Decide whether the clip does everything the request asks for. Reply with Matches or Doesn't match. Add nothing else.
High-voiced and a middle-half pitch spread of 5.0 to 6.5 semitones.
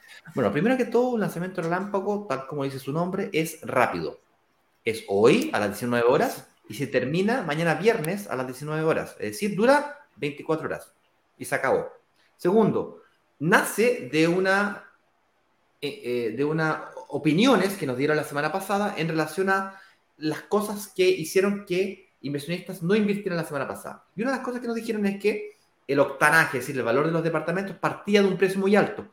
Doesn't match